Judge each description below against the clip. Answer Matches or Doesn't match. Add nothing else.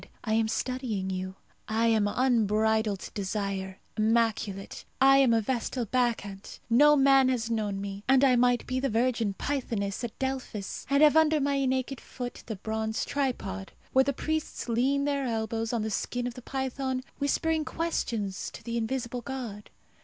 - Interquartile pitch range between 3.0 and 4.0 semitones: Matches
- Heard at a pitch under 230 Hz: Doesn't match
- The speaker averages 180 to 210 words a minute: Doesn't match